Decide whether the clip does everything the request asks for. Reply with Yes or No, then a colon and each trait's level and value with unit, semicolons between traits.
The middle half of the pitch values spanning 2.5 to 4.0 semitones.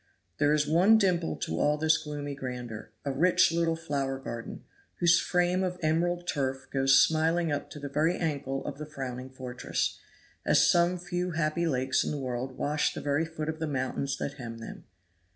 Yes: average, 3.7 semitones